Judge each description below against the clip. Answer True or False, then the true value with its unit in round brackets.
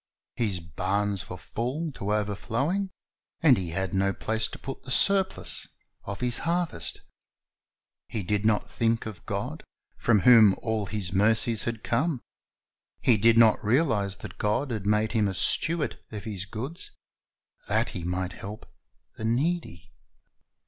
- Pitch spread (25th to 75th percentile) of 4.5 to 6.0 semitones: False (3.8 semitones)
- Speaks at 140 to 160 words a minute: True (150 wpm)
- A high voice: False (110 Hz)